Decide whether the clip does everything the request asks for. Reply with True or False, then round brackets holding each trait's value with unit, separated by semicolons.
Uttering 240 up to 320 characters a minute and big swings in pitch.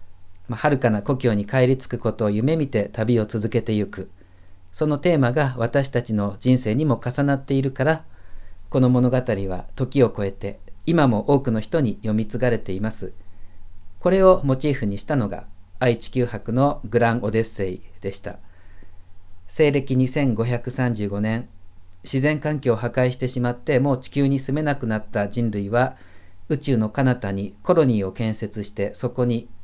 False (300 characters per minute; 4.7 semitones)